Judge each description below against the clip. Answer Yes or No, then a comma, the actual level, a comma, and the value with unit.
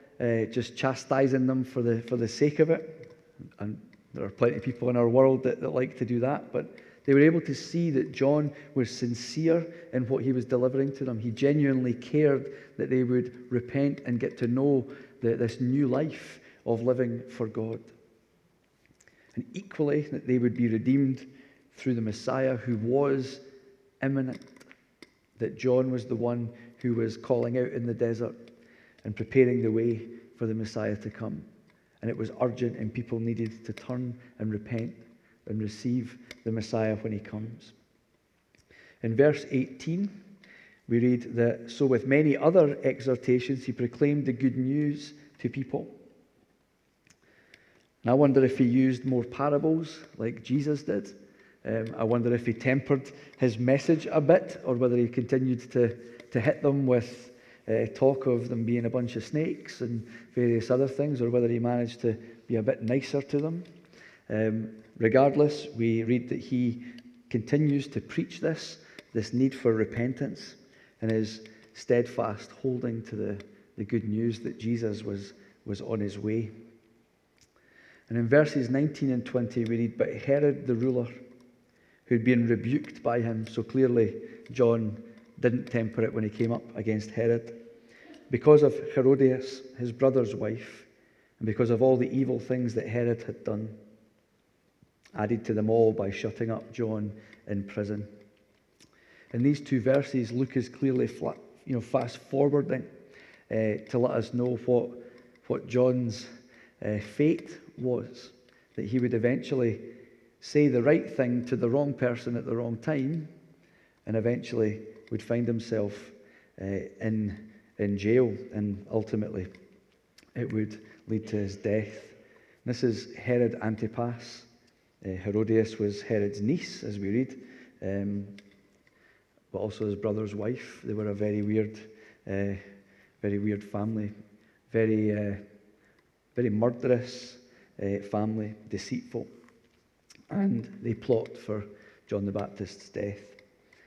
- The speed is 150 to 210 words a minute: Yes, average, 155 wpm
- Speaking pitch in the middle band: No, low, 120 Hz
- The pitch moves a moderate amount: Yes, average, 3.0 semitones